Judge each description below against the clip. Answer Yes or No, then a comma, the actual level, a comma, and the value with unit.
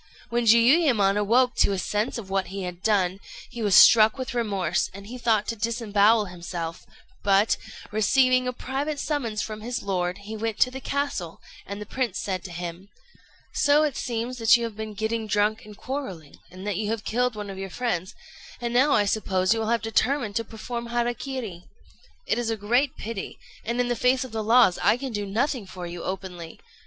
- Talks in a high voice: Yes, high, 220 Hz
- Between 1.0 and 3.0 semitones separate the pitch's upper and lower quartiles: No, average, 3.7 semitones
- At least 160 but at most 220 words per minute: Yes, fast, 205 wpm